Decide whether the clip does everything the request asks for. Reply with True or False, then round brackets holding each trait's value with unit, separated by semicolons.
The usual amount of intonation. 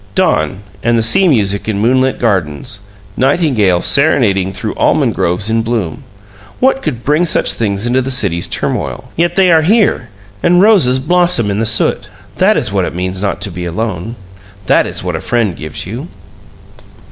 False (6.5 semitones)